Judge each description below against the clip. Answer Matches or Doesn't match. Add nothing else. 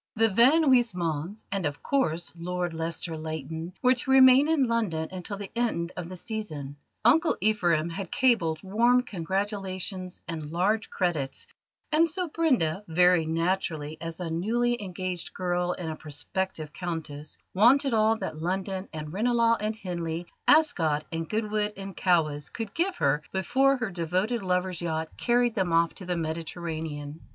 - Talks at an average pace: Matches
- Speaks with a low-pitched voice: Doesn't match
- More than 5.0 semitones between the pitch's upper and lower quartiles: Matches